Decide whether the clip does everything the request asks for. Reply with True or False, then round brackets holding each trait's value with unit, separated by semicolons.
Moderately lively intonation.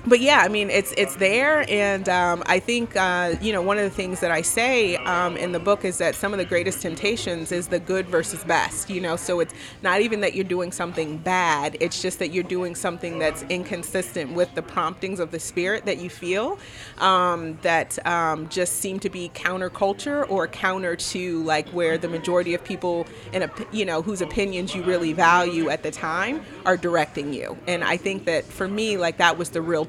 False (2.3 semitones)